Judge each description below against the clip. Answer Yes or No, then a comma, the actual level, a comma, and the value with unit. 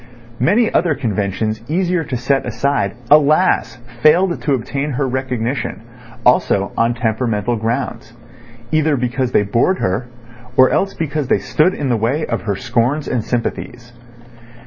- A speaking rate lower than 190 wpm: Yes, average, 140 wpm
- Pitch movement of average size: Yes, average, 4.2 semitones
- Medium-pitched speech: No, low, 125 Hz